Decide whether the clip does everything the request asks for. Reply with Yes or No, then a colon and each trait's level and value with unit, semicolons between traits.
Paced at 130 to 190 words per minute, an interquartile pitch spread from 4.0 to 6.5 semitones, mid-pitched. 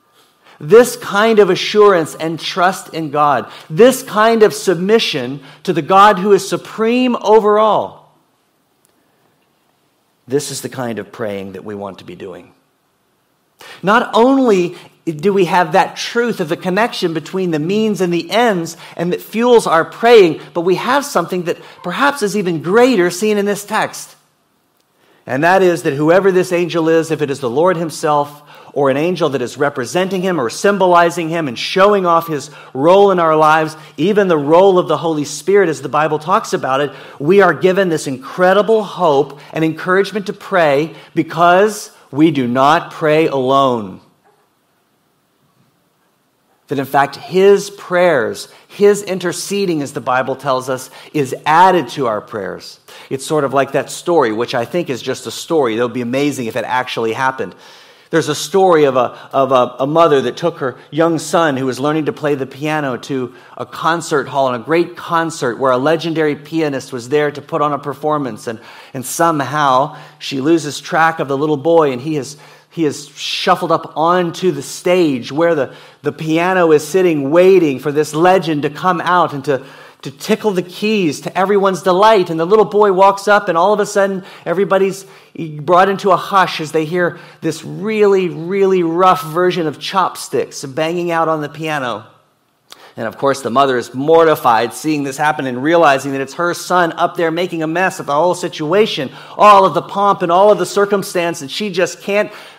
Yes: average, 185 wpm; average, 4.4 semitones; medium, 165 Hz